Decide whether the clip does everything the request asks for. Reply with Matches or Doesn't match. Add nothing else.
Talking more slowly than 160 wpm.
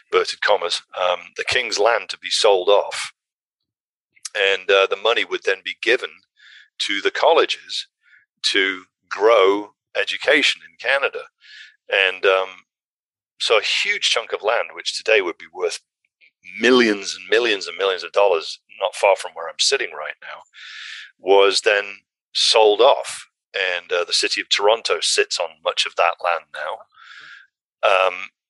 Matches